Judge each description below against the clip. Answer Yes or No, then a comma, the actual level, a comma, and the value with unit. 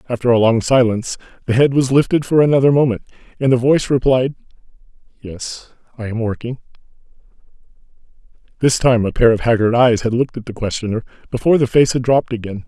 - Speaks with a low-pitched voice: Yes, low, 125 Hz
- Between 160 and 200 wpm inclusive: Yes, average, 170 wpm